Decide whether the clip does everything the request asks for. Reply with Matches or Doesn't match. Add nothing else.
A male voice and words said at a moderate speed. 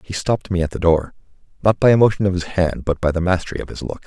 Doesn't match